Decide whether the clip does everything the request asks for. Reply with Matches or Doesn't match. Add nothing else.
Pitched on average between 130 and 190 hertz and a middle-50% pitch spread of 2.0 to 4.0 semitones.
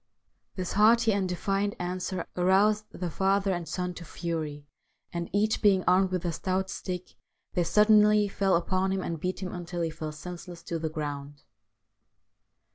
Matches